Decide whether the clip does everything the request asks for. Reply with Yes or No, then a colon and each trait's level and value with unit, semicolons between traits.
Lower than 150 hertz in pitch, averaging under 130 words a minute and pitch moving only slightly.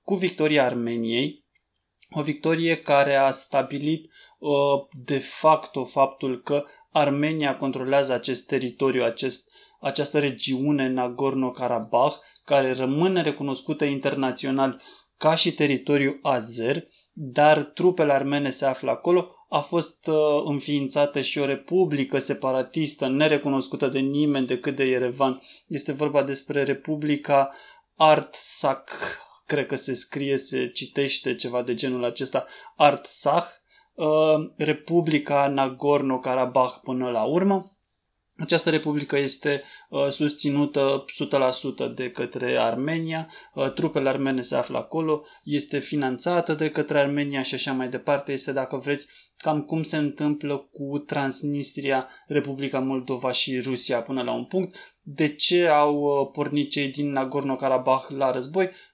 Yes: medium, 140 Hz; average, 120 wpm; narrow, 2.1 semitones